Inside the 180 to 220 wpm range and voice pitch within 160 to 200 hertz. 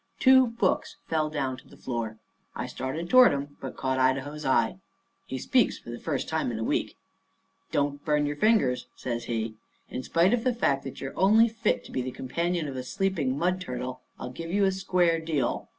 No: fast, 205 wpm; medium, 145 Hz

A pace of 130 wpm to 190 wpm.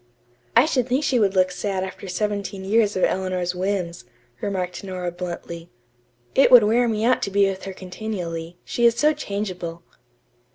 Yes: average, 170 wpm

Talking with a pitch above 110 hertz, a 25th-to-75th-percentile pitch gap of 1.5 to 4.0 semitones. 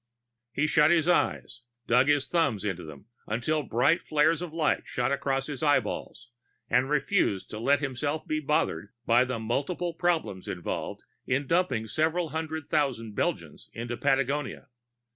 No: medium, 140 Hz; average, 4.6 semitones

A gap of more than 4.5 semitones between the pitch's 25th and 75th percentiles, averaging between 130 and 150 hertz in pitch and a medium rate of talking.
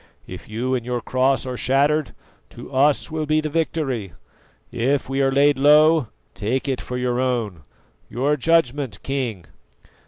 No: average, 3.1 semitones; low, 135 Hz; average, 155 wpm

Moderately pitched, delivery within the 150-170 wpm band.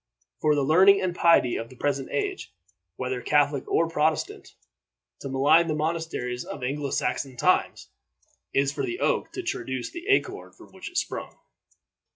Yes: medium, 150 Hz; average, 165 wpm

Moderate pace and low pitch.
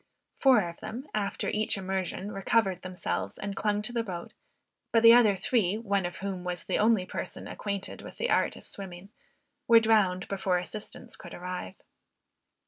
No: average, 170 wpm; high, 195 Hz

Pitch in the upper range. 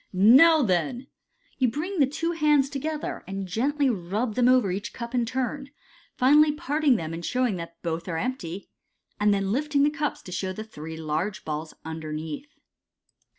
Yes: high, 235 Hz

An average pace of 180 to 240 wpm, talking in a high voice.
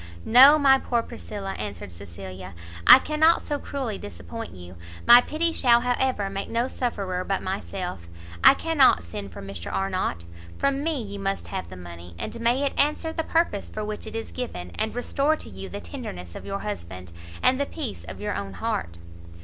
Yes: average, 190 wpm; high, 200 Hz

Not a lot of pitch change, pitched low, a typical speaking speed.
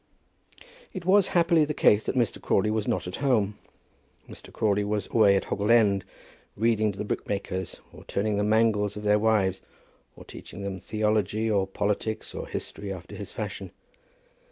Yes: narrow, 2.0 semitones; low, 105 Hz; average, 170 wpm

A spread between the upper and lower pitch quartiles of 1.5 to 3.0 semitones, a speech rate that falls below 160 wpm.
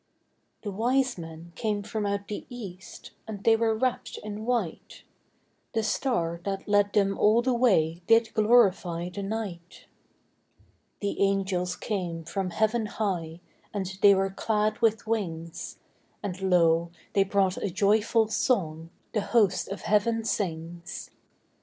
No: average, 3.7 semitones; average, 140 wpm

